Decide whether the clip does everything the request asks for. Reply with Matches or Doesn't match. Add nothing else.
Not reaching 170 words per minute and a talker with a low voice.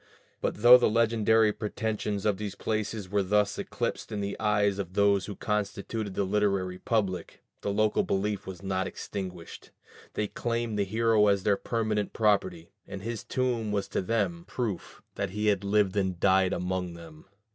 Doesn't match